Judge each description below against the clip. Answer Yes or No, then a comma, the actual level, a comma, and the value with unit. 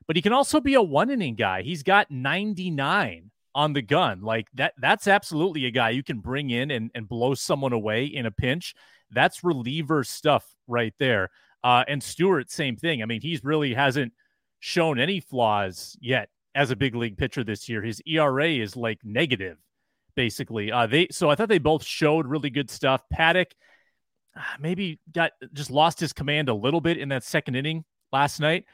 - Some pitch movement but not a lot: Yes, average, 5.0 semitones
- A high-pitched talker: No, medium, 140 Hz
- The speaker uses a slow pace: No, average, 190 wpm